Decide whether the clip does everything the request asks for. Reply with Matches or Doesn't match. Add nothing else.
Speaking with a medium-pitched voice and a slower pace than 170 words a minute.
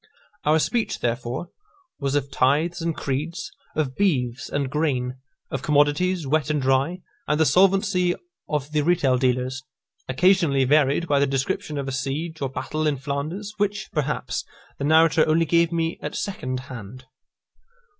Matches